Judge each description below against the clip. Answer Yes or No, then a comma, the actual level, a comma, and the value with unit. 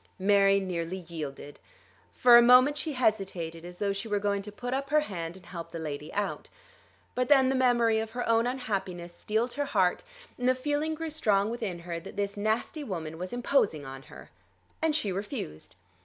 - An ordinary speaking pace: Yes, average, 195 wpm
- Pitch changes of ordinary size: No, wide, 5.9 semitones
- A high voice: Yes, high, 205 Hz